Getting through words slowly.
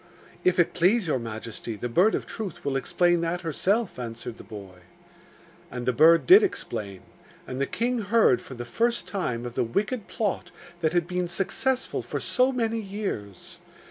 No: average, 175 wpm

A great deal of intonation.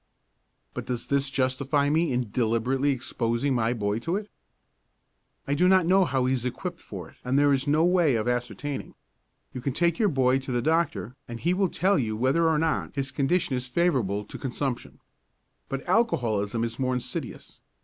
No: average, 4.7 semitones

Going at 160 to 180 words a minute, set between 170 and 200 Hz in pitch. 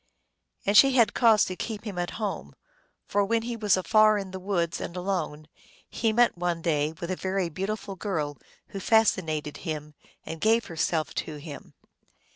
Yes: average, 175 wpm; high, 190 Hz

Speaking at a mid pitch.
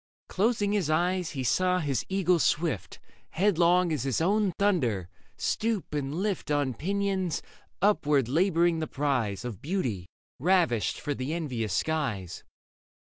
Yes: medium, 160 Hz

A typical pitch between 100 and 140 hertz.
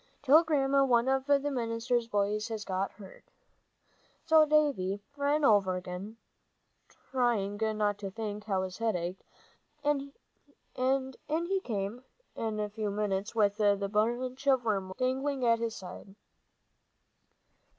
No: high, 225 Hz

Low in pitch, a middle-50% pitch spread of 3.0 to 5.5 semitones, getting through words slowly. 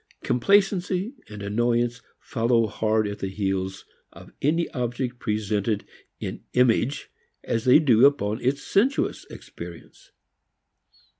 Yes: low, 120 Hz; average, 4.8 semitones; slow, 115 wpm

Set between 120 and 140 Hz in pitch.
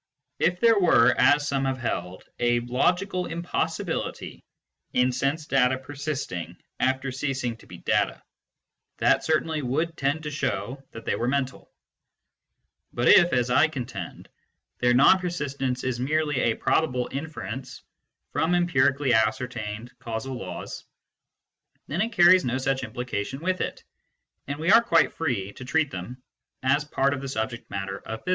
Yes: low, 135 Hz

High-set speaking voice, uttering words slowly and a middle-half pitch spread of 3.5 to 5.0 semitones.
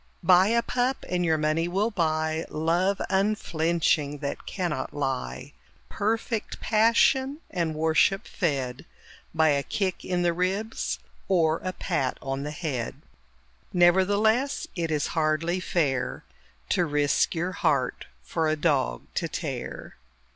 No: medium, 170 Hz; slow, 130 wpm; average, 3.9 semitones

